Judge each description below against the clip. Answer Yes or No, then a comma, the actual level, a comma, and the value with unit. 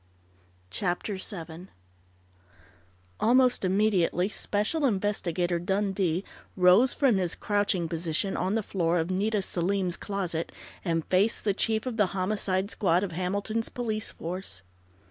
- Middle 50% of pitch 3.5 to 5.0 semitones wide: No, average, 3.1 semitones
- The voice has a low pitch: No, high, 190 Hz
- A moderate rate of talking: No, slow, 125 wpm